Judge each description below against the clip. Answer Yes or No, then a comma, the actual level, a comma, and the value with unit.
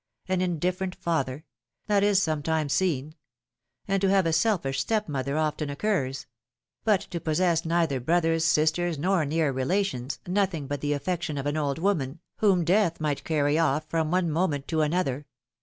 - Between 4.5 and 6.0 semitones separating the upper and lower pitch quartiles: No, average, 4.0 semitones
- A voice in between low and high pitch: Yes, medium, 160 Hz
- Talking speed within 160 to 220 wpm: Yes, average, 170 wpm